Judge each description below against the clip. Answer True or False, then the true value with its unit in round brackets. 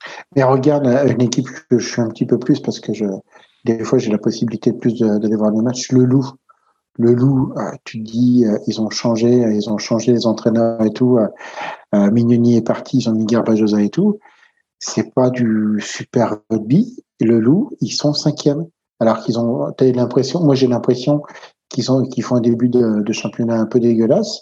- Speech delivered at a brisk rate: False (195 wpm)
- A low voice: True (120 Hz)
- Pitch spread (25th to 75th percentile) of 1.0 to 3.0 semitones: True (2.7 semitones)